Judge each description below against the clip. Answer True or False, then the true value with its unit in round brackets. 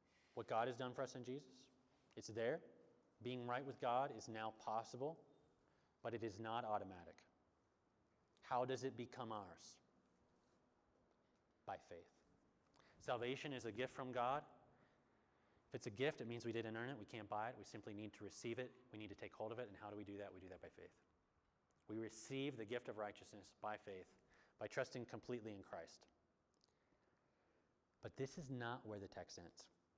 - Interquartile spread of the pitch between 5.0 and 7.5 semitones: False (3.0 semitones)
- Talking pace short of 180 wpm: False (190 wpm)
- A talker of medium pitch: False (115 Hz)